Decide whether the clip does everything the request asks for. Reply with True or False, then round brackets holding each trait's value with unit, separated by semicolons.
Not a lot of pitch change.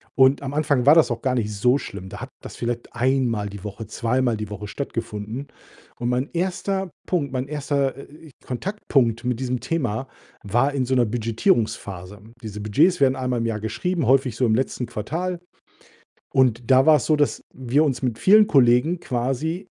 False (4.0 semitones)